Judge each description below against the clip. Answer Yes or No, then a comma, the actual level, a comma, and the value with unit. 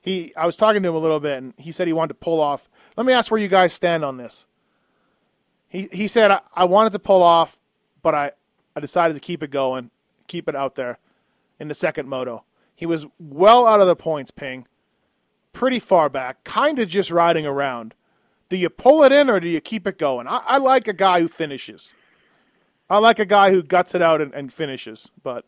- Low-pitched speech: No, medium, 170 Hz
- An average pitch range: No, wide, 5.7 semitones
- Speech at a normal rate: No, fast, 230 wpm